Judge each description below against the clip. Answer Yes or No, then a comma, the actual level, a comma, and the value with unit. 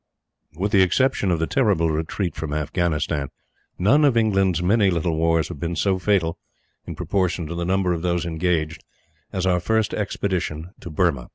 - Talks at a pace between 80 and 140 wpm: No, average, 175 wpm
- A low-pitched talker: Yes, very low, 85 Hz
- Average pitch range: Yes, average, 3.0 semitones